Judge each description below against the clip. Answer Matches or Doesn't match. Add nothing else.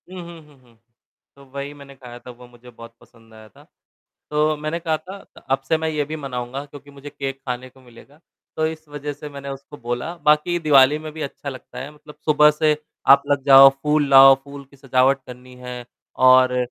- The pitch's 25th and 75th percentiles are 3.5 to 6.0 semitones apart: Doesn't match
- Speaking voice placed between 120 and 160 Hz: Matches